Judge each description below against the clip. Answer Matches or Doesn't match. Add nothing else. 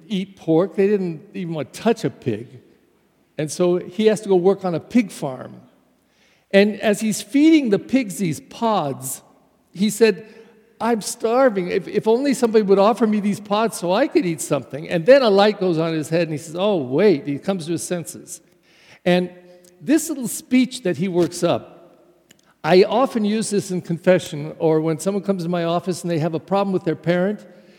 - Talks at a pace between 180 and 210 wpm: Matches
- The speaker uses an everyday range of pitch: Matches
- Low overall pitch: Doesn't match